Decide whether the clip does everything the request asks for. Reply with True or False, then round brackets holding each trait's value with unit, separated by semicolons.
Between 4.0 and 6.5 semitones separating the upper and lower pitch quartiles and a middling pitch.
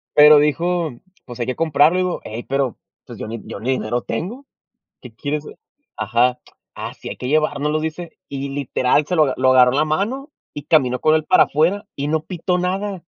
True (4.6 semitones; 150 Hz)